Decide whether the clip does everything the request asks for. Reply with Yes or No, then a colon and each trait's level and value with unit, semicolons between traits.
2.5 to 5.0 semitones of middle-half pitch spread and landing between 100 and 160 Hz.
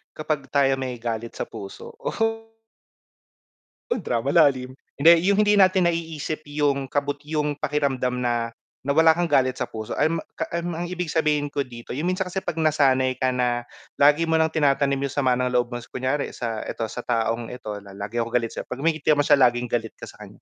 Yes: average, 4.6 semitones; medium, 140 Hz